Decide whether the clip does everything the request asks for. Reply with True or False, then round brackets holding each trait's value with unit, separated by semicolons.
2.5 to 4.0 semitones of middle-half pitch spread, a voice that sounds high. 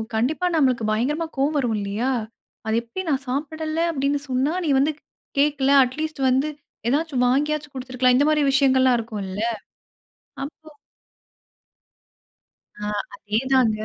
True (3.4 semitones; 270 Hz)